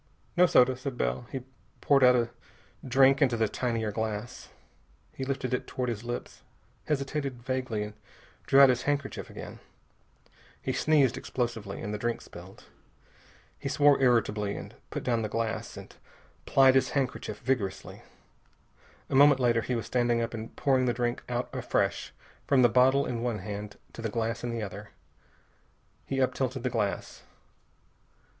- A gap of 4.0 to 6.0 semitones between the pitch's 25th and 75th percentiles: No, average, 2.8 semitones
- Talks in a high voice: No, low, 125 Hz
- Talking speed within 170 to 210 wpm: No, average, 160 wpm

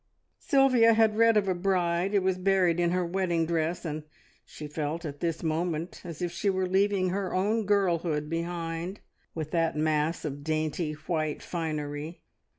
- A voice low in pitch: No, medium, 170 Hz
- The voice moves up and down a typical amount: Yes, average, 3.2 semitones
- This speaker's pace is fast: No, average, 165 wpm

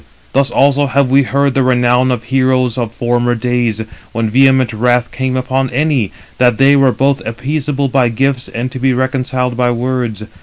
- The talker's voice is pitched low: Yes, low, 130 Hz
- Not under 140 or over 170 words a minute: No, average, 180 wpm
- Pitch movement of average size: No, narrow, 1.8 semitones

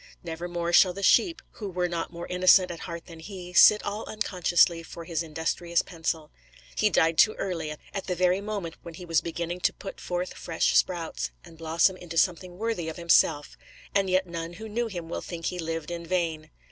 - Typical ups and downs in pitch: No, narrow, 1.9 semitones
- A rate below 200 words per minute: No, fast, 205 wpm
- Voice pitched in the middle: Yes, medium, 175 Hz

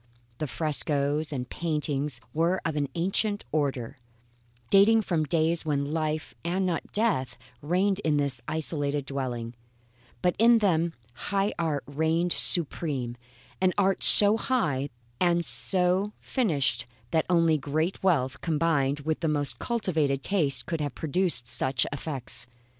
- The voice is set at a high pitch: No, medium, 155 Hz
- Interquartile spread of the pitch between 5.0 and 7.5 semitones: No, average, 4.2 semitones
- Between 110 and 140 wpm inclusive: Yes, slow, 135 wpm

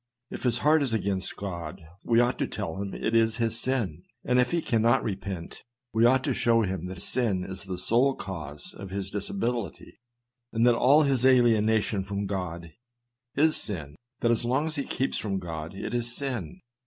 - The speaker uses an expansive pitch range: No, average, 4.5 semitones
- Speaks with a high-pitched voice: No, low, 110 Hz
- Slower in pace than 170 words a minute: No, average, 195 wpm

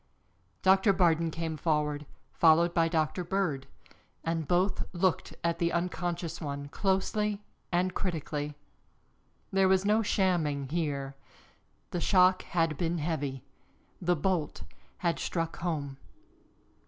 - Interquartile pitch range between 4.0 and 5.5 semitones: No, average, 3.2 semitones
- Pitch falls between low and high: Yes, medium, 170 Hz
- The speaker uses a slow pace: Yes, slow, 115 wpm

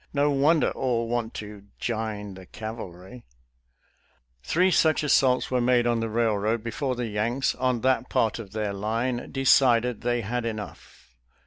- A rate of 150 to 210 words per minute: Yes, average, 165 wpm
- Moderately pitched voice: No, low, 115 Hz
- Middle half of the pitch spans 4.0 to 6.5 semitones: No, average, 2.8 semitones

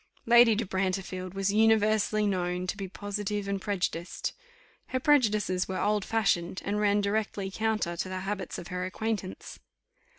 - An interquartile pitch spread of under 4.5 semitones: Yes, narrow, 2.4 semitones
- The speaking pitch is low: No, high, 200 Hz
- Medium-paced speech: Yes, average, 160 wpm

